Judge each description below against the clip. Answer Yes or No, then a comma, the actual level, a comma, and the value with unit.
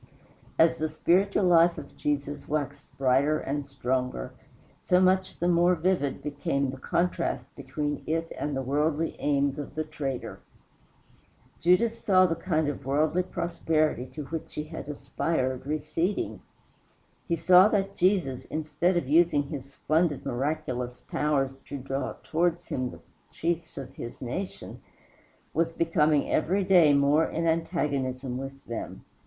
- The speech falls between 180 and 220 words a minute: No, average, 140 wpm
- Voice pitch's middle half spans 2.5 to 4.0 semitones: Yes, average, 3.7 semitones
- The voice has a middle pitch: Yes, medium, 155 Hz